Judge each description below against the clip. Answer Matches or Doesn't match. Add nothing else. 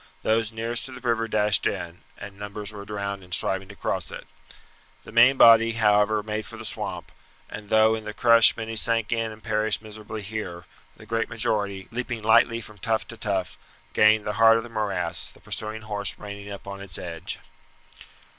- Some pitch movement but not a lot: Doesn't match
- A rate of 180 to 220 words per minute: Matches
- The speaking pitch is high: Doesn't match